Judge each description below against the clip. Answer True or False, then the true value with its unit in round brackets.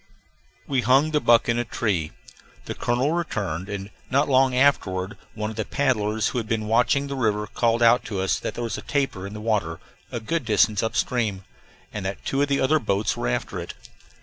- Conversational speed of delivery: False (215 wpm)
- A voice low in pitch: True (115 Hz)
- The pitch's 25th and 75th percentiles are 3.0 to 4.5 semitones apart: True (4.1 semitones)